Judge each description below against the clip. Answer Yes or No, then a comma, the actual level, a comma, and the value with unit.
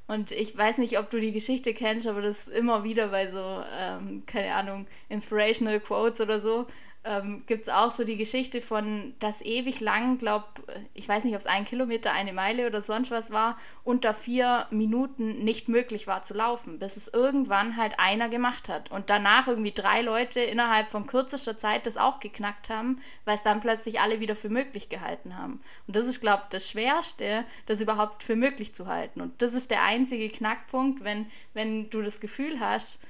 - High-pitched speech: Yes, high, 220 Hz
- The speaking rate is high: Yes, fast, 200 wpm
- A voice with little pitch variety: Yes, narrow, 2.3 semitones